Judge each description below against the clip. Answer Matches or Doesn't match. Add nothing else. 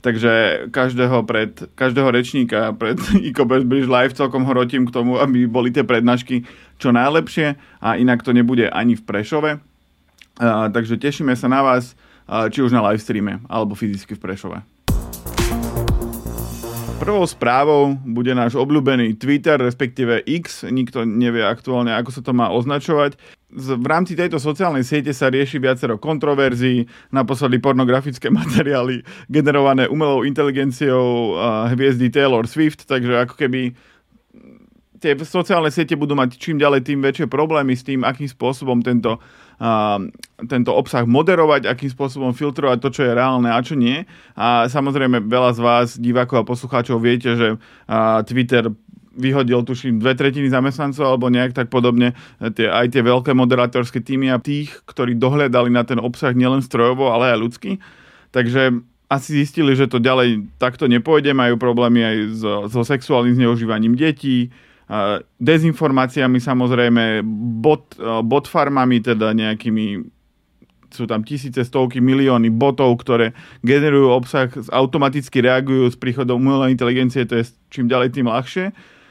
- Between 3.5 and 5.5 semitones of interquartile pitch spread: Doesn't match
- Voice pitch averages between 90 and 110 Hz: Doesn't match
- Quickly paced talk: Doesn't match